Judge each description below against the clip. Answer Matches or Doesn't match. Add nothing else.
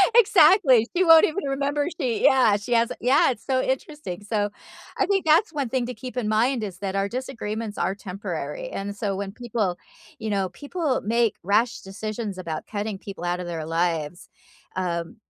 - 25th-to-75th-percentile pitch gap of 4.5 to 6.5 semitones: Matches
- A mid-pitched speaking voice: Doesn't match